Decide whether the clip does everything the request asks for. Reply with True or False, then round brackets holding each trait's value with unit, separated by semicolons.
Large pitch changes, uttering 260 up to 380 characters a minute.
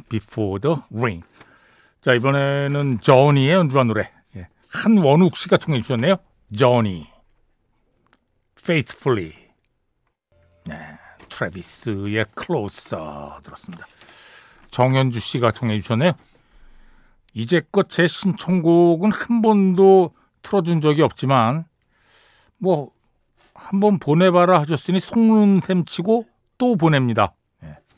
False (8.3 semitones; 245 characters per minute)